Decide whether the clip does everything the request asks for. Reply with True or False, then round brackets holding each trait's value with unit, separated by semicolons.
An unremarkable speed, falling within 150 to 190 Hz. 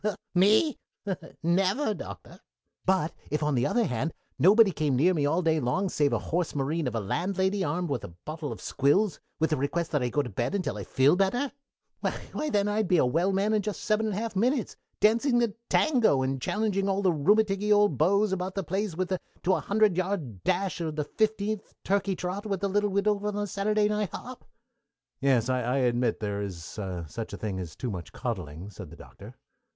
False (210 wpm; 185 Hz)